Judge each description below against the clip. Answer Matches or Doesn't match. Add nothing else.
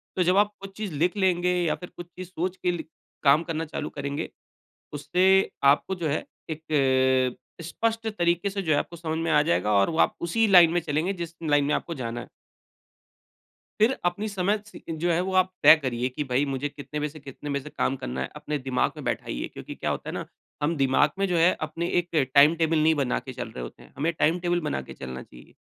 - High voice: Doesn't match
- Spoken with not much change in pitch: Doesn't match